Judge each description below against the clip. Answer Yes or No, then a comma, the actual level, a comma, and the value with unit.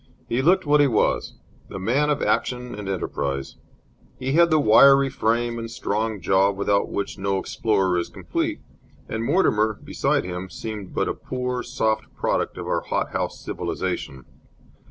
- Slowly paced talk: No, average, 160 wpm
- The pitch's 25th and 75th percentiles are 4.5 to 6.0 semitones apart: Yes, average, 4.9 semitones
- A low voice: Yes, low, 110 Hz